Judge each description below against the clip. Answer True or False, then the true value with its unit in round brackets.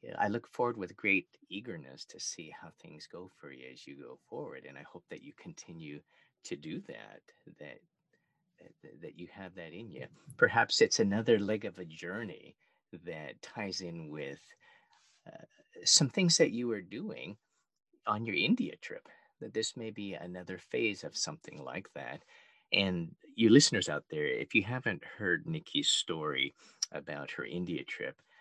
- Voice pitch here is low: True (115 Hz)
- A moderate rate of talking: True (170 wpm)